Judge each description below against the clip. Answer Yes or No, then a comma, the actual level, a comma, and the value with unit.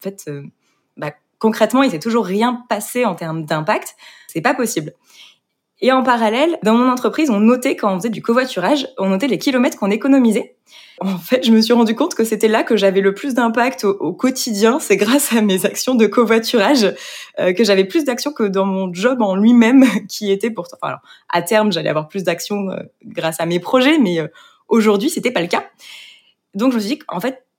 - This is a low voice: No, high, 225 Hz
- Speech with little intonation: No, average, 4.3 semitones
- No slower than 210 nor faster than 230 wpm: Yes, average, 215 wpm